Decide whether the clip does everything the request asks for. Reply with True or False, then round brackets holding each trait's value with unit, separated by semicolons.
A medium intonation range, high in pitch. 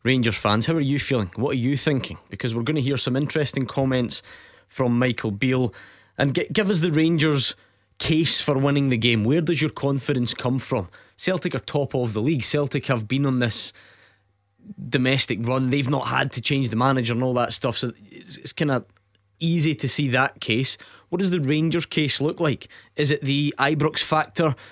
False (3.7 semitones; 135 Hz)